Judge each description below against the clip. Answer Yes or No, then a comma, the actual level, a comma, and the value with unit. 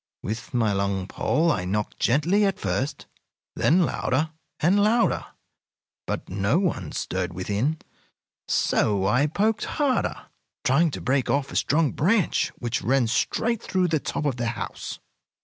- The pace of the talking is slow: No, average, 150 wpm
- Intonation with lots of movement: Yes, wide, 8.4 semitones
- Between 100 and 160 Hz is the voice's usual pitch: Yes, medium, 140 Hz